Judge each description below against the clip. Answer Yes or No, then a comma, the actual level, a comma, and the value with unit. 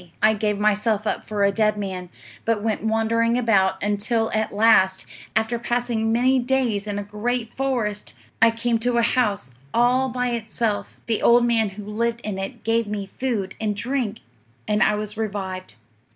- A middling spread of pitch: No, narrow, 2.3 semitones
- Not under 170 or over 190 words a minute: Yes, average, 175 wpm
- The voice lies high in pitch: Yes, high, 220 Hz